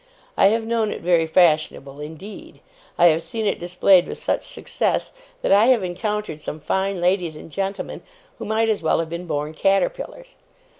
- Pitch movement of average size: Yes, average, 4.6 semitones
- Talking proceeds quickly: No, average, 180 wpm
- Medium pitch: Yes, medium, 180 Hz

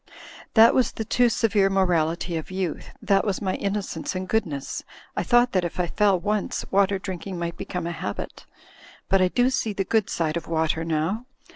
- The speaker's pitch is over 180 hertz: Yes, high, 190 Hz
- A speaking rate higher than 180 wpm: Yes, average, 195 wpm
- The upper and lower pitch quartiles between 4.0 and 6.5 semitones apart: No, average, 3.6 semitones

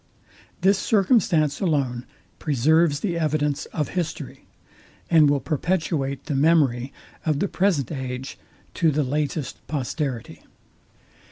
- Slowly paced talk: Yes, slow, 110 wpm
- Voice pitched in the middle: Yes, medium, 150 Hz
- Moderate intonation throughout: Yes, average, 3.4 semitones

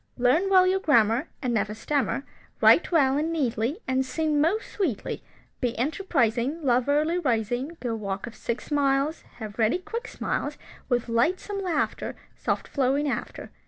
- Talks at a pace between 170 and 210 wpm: No, average, 155 wpm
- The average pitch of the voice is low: No, very high, 275 Hz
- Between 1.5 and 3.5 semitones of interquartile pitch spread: No, wide, 5.5 semitones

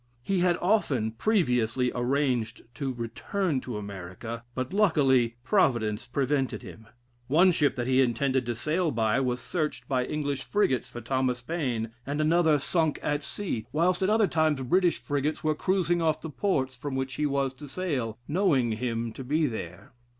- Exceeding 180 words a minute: No, average, 170 wpm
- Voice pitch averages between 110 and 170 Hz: Yes, low, 135 Hz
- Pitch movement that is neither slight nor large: Yes, average, 4.8 semitones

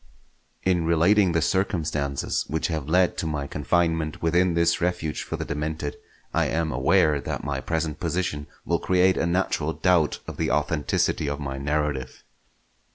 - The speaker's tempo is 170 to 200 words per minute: No, average, 160 wpm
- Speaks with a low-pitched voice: Yes, very low, 80 Hz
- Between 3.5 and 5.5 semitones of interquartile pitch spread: No, average, 2.9 semitones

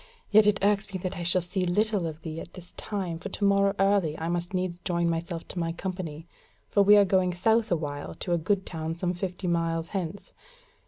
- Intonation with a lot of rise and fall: No, average, 2.9 semitones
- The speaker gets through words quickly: Yes, fast, 225 wpm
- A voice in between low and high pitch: Yes, medium, 180 Hz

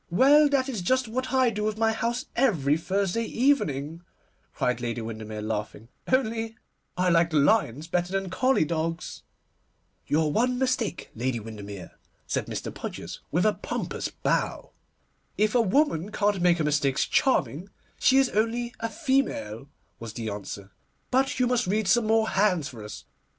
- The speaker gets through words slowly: No, average, 160 wpm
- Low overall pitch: No, high, 195 Hz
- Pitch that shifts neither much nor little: No, wide, 9.0 semitones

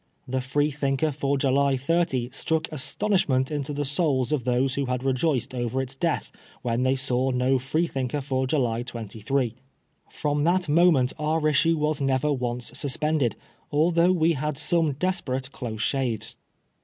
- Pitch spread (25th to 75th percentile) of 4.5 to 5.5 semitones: No, average, 3.1 semitones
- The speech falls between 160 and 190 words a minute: No, average, 150 wpm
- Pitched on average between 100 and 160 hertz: Yes, low, 135 Hz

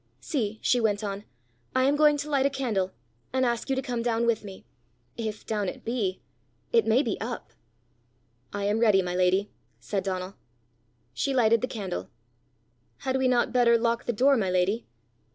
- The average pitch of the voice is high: Yes, high, 230 Hz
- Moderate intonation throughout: Yes, average, 4.1 semitones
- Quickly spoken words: No, average, 185 wpm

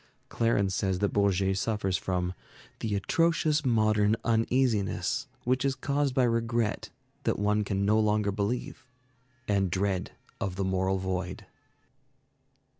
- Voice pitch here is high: No, low, 105 Hz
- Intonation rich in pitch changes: No, average, 3.4 semitones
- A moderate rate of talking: No, slow, 125 wpm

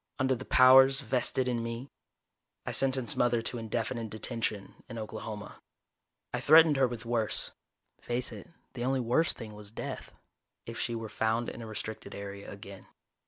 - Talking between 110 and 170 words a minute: Yes, average, 165 wpm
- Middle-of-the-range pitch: No, low, 115 Hz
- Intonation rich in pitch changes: No, average, 2.9 semitones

